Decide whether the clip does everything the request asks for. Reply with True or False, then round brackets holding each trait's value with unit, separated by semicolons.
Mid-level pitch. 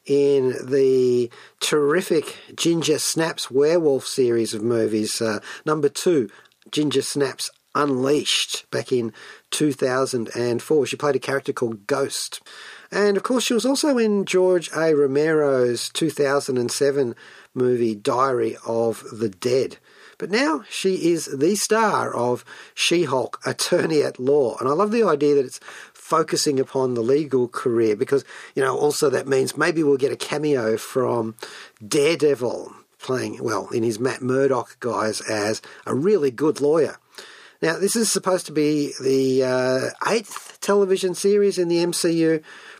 True (145 Hz)